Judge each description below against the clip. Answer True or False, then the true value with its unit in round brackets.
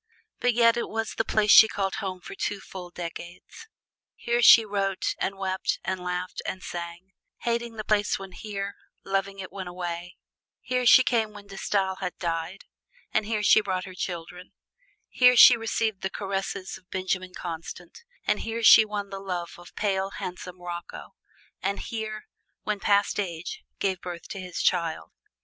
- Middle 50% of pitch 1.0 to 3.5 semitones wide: True (2.9 semitones)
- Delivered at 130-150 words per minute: False (170 wpm)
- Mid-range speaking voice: False (195 Hz)